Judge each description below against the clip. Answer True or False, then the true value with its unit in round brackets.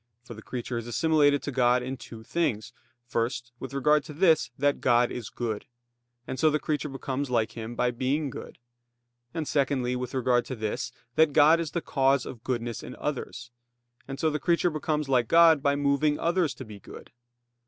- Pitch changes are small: False (3.7 semitones)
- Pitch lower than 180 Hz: True (135 Hz)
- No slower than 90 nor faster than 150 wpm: False (195 wpm)